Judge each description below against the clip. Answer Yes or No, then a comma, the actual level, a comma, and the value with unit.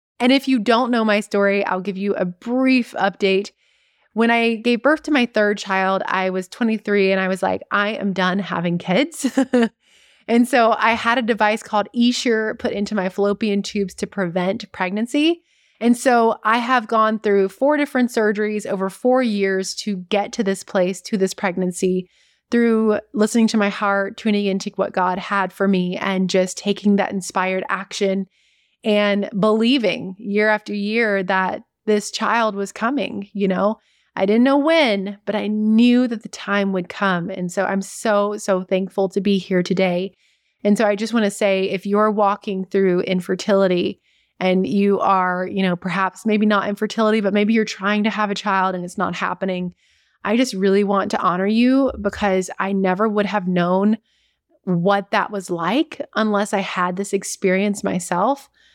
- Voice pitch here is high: Yes, high, 205 Hz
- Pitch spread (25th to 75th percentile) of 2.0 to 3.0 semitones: Yes, narrow, 2.5 semitones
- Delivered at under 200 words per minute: Yes, average, 180 wpm